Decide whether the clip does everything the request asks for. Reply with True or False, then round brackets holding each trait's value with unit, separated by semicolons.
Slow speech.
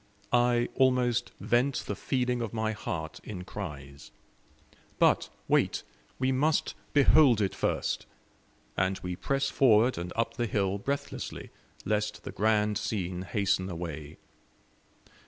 True (125 wpm)